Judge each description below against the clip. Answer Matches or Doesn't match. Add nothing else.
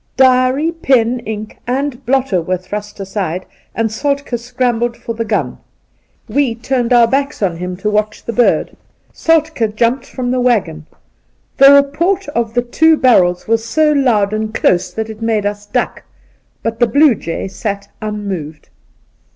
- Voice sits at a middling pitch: Doesn't match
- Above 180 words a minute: Doesn't match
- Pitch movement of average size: Matches